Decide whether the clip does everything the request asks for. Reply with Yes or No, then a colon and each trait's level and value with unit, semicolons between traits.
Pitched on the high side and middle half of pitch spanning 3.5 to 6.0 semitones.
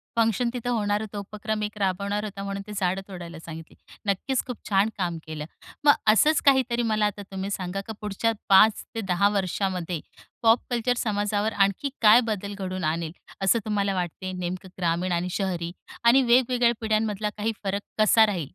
No: high, 205 Hz; average, 2.9 semitones